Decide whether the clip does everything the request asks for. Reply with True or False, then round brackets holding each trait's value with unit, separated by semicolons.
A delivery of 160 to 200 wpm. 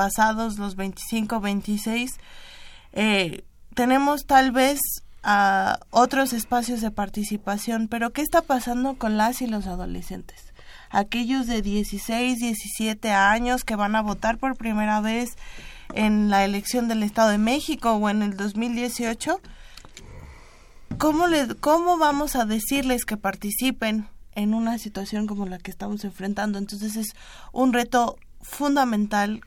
False (135 wpm)